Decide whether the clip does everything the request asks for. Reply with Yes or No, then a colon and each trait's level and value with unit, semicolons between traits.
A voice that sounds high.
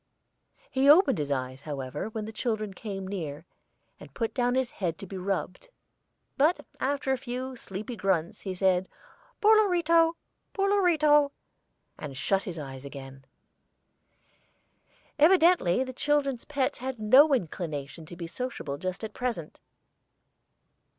Yes: high, 220 Hz